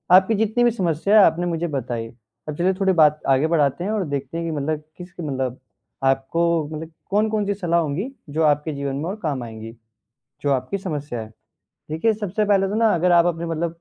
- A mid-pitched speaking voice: Yes, medium, 165 Hz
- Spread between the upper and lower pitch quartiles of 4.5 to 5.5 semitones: Yes, average, 5.1 semitones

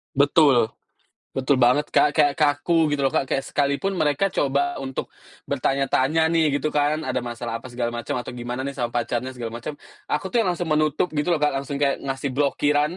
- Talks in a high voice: No, medium, 140 Hz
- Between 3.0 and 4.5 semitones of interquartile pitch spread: No, narrow, 2.6 semitones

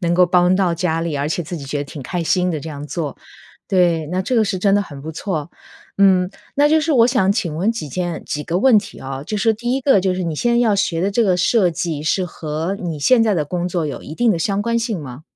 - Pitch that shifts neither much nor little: Yes, average, 4.3 semitones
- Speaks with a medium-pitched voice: Yes, medium, 180 Hz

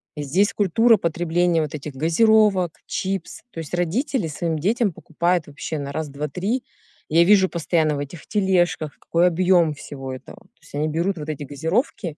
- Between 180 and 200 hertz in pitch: No, medium, 170 Hz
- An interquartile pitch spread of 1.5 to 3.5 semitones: No, average, 3.9 semitones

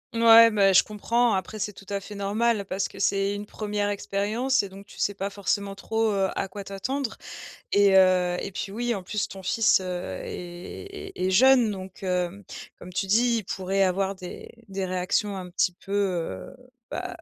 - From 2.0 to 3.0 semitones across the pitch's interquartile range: Yes, narrow, 2.4 semitones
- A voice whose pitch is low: No, high, 200 Hz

